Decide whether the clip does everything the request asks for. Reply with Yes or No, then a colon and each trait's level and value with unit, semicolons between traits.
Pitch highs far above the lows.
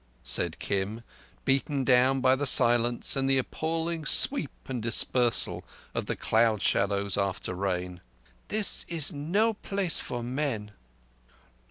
Yes: wide, 5.7 semitones